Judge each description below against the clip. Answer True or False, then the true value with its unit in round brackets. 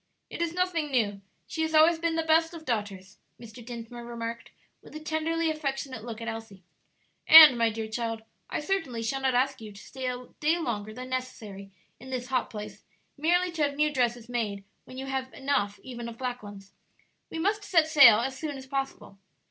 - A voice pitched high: True (255 Hz)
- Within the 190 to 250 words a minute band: True (200 wpm)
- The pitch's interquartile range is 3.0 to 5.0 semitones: False (5.4 semitones)